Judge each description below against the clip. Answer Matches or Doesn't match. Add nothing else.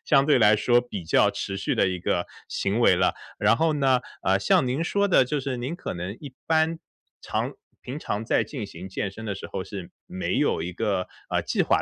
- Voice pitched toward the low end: Matches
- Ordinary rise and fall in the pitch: Doesn't match